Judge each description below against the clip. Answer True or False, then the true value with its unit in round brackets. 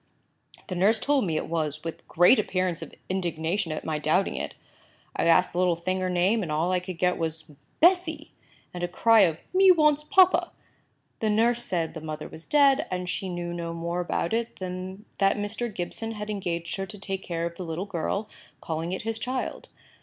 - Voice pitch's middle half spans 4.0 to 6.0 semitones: True (4.5 semitones)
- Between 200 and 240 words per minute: True (205 wpm)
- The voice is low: False (185 Hz)